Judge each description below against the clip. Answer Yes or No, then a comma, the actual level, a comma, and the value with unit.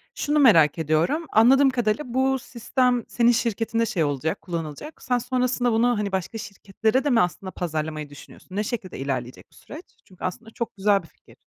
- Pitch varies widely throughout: Yes, wide, 6.3 semitones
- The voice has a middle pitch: No, high, 220 Hz